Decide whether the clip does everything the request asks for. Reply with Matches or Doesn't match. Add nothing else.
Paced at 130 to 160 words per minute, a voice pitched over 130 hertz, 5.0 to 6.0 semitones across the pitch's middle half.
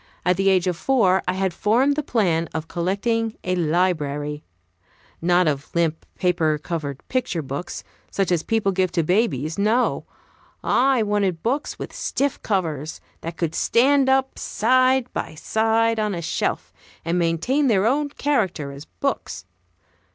Matches